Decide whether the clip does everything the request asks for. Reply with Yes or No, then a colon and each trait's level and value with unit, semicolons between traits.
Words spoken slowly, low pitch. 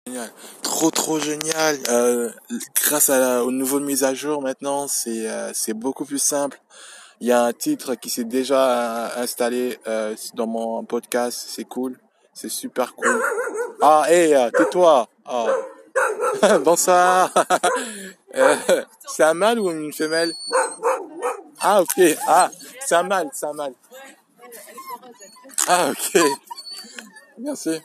No: slow, 135 wpm; medium, 160 Hz